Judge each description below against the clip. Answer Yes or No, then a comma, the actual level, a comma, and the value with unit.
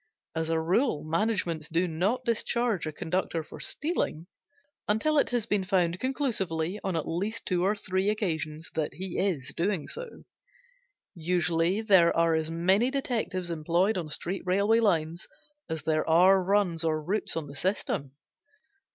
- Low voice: No, medium, 180 Hz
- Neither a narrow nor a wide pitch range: Yes, average, 4.2 semitones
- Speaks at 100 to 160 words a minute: Yes, average, 155 wpm